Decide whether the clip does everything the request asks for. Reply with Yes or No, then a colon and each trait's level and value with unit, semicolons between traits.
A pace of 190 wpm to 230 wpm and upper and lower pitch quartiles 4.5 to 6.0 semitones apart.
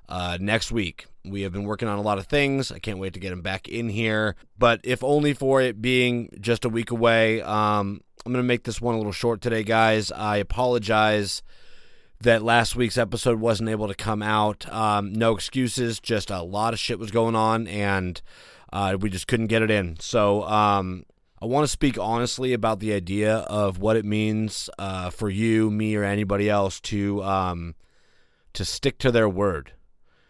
No: average, 200 wpm; narrow, 2.6 semitones